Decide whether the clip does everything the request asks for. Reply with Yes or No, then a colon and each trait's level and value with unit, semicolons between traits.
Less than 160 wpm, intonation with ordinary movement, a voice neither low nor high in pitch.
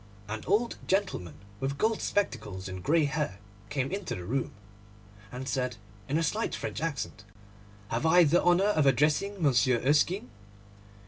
No: average, 150 wpm; wide, 6.0 semitones; medium, 145 Hz